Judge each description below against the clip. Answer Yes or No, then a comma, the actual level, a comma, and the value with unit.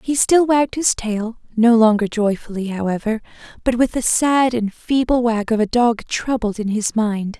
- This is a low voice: No, high, 230 Hz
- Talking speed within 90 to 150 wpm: No, average, 180 wpm